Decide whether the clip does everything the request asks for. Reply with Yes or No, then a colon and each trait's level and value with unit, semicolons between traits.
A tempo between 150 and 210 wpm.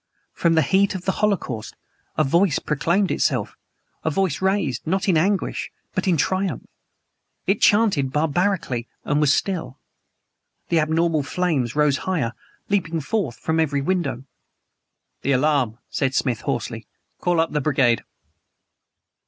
No: slow, 135 wpm